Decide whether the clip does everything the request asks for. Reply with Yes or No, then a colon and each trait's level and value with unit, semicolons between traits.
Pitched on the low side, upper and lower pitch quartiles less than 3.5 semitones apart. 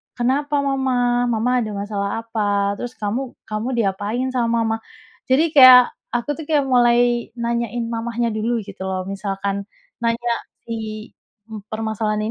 No: high, 230 Hz; average, 2.7 semitones